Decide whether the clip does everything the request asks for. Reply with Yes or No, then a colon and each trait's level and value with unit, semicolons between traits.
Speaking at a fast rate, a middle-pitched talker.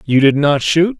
Yes: fast, 240 wpm; medium, 150 Hz